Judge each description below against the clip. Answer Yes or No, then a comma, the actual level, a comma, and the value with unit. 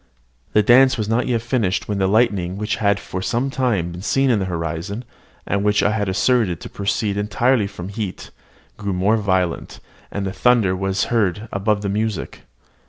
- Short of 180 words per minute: No, average, 185 wpm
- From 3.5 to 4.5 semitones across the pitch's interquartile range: No, average, 3.0 semitones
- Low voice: Yes, low, 105 Hz